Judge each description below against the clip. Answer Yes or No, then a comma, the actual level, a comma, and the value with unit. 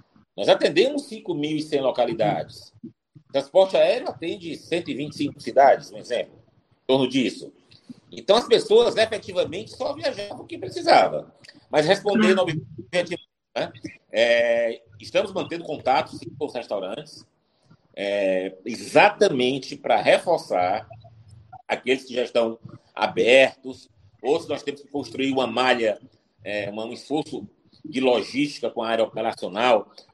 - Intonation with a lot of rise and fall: Yes, wide, 7.5 semitones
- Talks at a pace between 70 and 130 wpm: Yes, average, 125 wpm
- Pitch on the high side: No, low, 130 Hz